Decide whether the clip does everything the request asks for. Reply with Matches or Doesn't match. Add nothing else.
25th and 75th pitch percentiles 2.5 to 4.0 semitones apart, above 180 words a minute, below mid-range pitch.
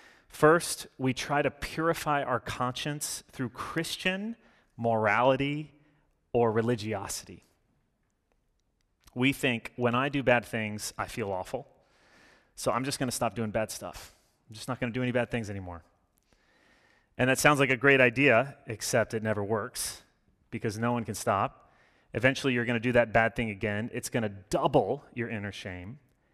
Doesn't match